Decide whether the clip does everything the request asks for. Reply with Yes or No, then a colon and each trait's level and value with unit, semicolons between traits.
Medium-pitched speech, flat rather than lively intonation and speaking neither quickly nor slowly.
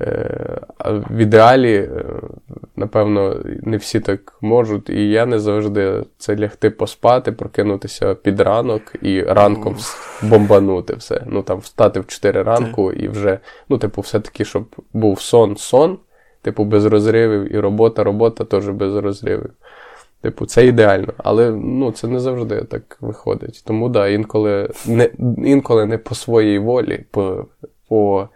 No: low, 110 Hz; narrow, 2.0 semitones; average, 140 wpm